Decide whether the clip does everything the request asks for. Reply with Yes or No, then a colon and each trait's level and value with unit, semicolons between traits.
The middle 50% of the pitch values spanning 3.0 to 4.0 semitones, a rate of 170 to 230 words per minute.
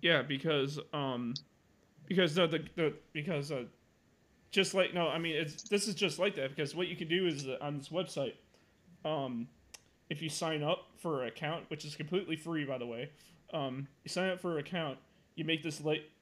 Yes: average, 3.3 semitones; fast, 205 wpm